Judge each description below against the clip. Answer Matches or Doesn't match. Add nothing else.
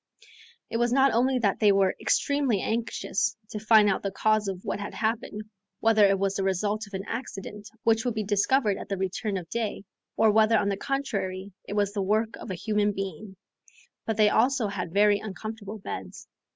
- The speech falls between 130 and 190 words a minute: Doesn't match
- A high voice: Matches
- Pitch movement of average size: Doesn't match